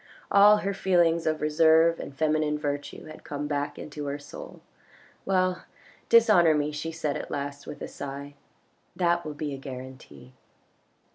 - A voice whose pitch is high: No, medium, 150 Hz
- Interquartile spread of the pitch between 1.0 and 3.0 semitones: Yes, average, 2.7 semitones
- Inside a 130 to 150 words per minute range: No, average, 165 wpm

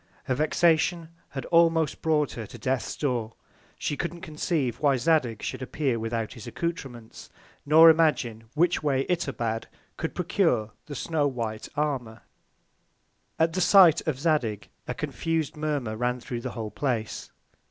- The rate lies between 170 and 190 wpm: No, average, 145 wpm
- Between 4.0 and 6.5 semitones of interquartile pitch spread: Yes, wide, 5.4 semitones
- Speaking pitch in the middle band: Yes, medium, 145 Hz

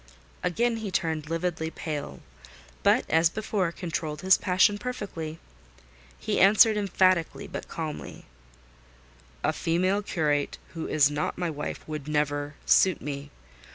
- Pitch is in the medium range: Yes, medium, 165 Hz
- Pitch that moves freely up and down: No, average, 4.1 semitones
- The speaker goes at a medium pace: No, slow, 125 wpm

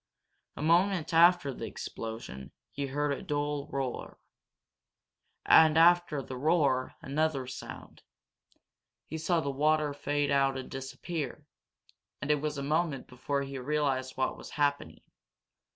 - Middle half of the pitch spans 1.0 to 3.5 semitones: Yes, narrow, 2.5 semitones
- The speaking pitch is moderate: Yes, medium, 145 Hz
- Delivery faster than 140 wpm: No, slow, 135 wpm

